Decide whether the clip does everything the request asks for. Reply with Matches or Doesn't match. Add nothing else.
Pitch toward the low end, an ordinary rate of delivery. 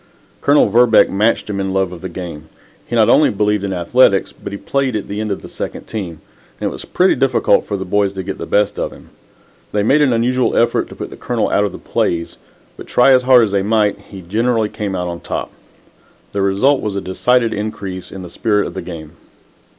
Doesn't match